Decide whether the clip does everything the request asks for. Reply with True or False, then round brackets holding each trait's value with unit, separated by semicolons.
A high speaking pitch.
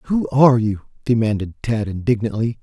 False (115 Hz)